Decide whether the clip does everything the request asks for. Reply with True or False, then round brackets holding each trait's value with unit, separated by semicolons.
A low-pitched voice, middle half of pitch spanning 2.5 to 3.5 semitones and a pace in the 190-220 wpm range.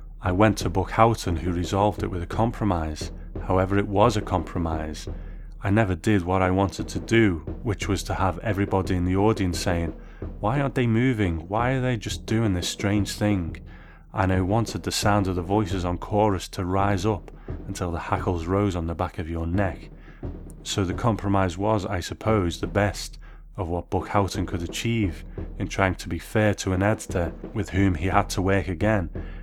True (95 Hz; 2.9 semitones; 200 wpm)